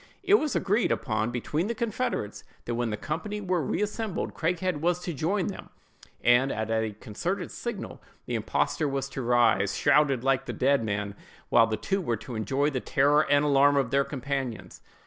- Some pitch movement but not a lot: No, wide, 7.0 semitones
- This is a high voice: No, medium, 140 Hz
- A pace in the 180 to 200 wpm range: Yes, average, 185 wpm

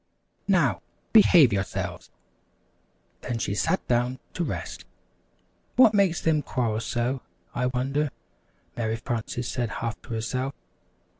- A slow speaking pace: Yes, slow, 120 wpm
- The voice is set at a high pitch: No, low, 125 Hz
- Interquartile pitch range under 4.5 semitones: Yes, average, 4.1 semitones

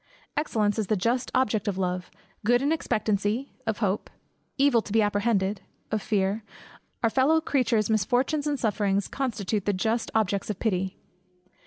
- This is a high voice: Yes, high, 215 Hz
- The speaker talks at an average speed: Yes, average, 155 wpm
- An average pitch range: Yes, average, 3.3 semitones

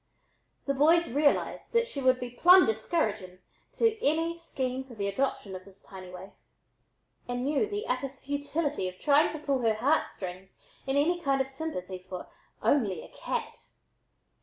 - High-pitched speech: Yes, very high, 270 Hz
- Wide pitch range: Yes, wide, 7.1 semitones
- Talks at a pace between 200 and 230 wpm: No, average, 160 wpm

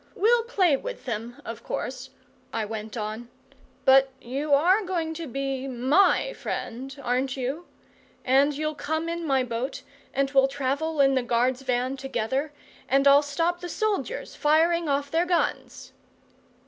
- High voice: Yes, very high, 275 Hz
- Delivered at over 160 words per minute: No, average, 150 wpm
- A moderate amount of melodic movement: Yes, average, 4.0 semitones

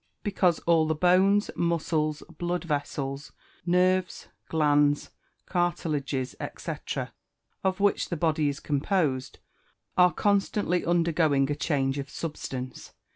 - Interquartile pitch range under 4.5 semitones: Yes, average, 3.5 semitones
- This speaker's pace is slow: Yes, slow, 115 wpm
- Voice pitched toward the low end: No, medium, 160 Hz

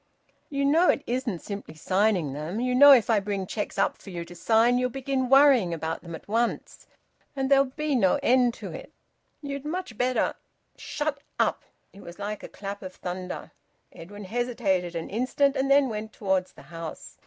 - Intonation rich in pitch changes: Yes, wide, 6.1 semitones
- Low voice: No, high, 225 Hz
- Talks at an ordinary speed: Yes, average, 195 wpm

